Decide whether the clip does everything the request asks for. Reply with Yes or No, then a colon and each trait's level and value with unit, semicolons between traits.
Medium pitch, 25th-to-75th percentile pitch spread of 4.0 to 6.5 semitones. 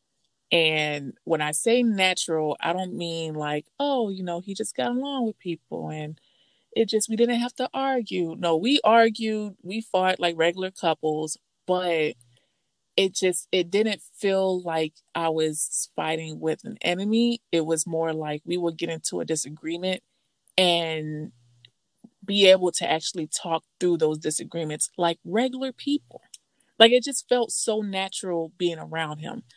Yes: medium, 175 Hz; wide, 5.4 semitones